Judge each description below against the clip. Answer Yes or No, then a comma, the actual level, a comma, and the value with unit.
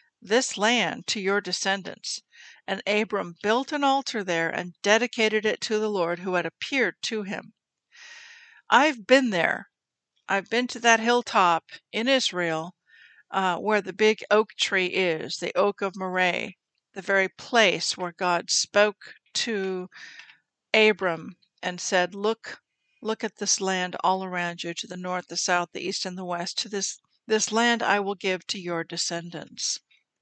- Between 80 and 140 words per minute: No, average, 160 wpm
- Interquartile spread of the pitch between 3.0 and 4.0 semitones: Yes, average, 3.5 semitones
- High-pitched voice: Yes, high, 200 Hz